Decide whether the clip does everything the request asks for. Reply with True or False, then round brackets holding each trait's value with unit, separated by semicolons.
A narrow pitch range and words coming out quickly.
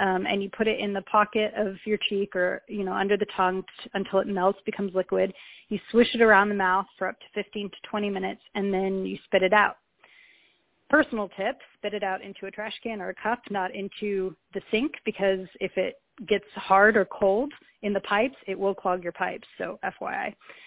True (1.8 semitones; 220 wpm)